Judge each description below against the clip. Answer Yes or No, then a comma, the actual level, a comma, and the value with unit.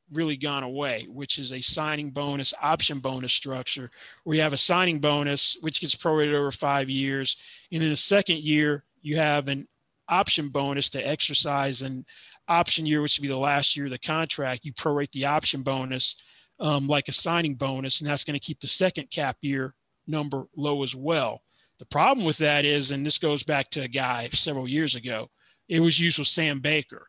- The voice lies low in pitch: No, medium, 145 Hz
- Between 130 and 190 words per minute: No, average, 200 wpm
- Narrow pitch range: Yes, narrow, 2.0 semitones